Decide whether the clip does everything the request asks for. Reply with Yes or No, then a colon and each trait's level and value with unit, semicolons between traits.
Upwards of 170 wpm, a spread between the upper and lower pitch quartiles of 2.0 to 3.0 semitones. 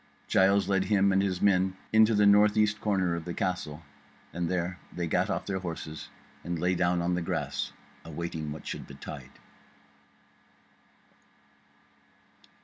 No: average, 145 wpm; narrow, 2.5 semitones